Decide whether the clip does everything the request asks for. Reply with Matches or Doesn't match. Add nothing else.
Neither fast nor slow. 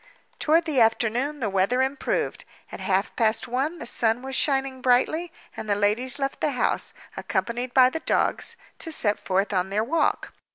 Matches